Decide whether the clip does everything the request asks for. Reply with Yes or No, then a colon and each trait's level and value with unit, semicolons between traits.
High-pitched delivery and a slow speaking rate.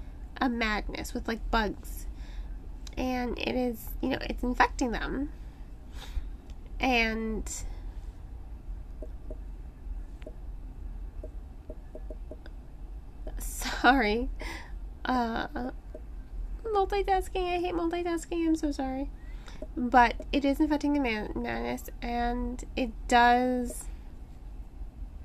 Yes: high, 220 Hz; slow, 80 wpm